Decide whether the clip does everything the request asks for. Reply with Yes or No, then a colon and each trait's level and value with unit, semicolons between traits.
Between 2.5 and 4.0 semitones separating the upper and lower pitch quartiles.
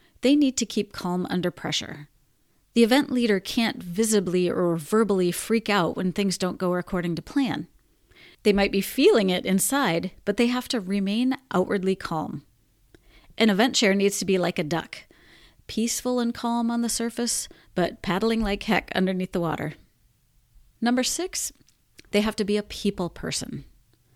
No: average, 4.6 semitones